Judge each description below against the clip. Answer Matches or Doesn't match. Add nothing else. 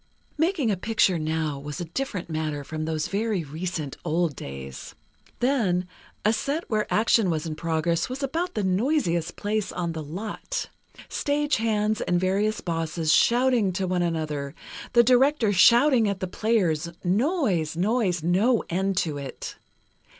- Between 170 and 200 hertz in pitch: Matches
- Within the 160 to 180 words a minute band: Doesn't match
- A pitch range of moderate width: Doesn't match